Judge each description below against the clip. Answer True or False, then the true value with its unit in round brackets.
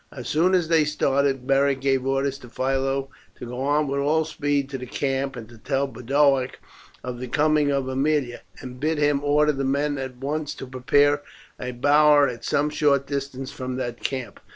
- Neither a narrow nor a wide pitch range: False (2.0 semitones)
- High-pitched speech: False (140 Hz)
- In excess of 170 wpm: True (195 wpm)